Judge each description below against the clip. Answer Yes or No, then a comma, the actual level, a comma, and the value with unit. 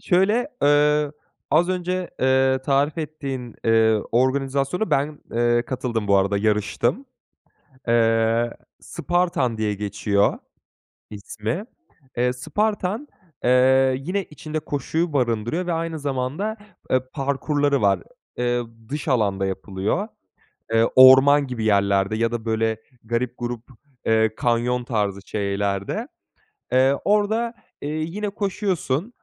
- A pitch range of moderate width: No, wide, 5.7 semitones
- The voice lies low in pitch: Yes, low, 130 Hz